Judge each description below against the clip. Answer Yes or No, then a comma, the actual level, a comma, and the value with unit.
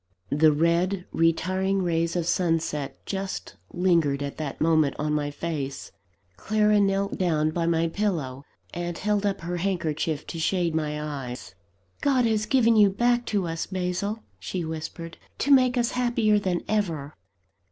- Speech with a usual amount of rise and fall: Yes, average, 4.2 semitones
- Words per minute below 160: Yes, average, 150 wpm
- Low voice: No, medium, 175 Hz